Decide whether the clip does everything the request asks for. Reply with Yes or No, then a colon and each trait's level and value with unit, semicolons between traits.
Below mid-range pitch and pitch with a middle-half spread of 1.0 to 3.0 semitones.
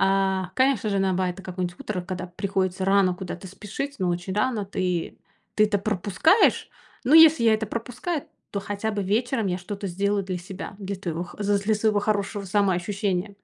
No: high, 200 Hz; narrow, 2.4 semitones